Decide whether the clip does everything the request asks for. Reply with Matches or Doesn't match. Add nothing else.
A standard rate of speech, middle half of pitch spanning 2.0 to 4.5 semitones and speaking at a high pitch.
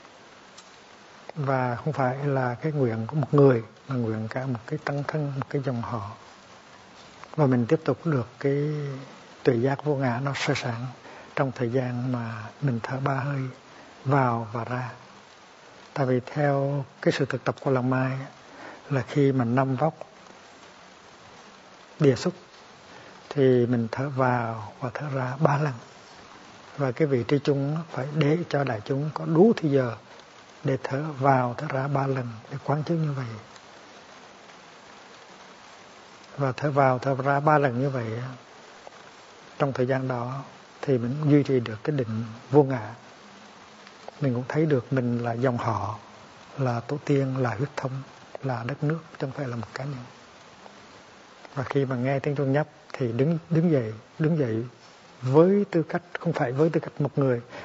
Doesn't match